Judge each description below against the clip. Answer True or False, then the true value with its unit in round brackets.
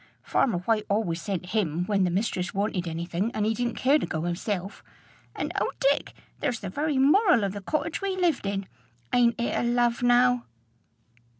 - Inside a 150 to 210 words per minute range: True (190 wpm)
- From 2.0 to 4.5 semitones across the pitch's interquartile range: False (4.9 semitones)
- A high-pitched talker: True (215 Hz)